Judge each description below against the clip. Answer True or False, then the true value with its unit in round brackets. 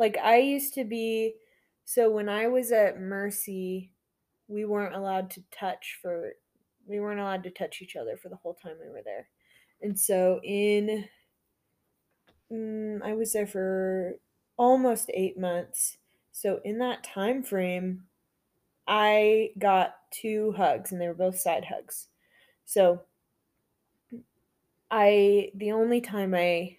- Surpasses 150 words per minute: False (140 wpm)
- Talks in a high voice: True (205 Hz)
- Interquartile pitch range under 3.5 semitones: True (2.9 semitones)